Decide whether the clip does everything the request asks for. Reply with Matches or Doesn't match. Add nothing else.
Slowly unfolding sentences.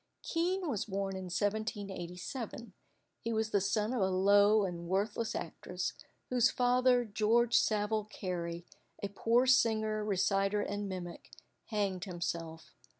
Matches